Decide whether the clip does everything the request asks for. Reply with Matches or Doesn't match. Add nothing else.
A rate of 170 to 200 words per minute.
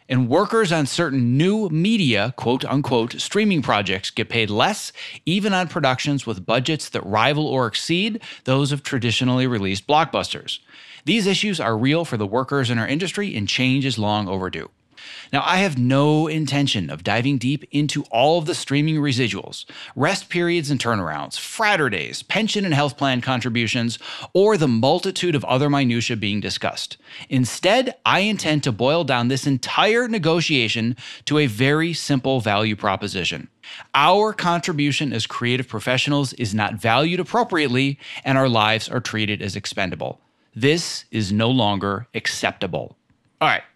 Doesn't match